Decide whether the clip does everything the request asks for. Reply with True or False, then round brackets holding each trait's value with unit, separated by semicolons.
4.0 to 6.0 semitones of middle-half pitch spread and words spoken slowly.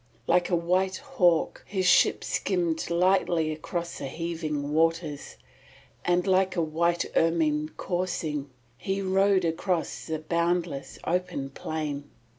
False (2.5 semitones; 120 wpm)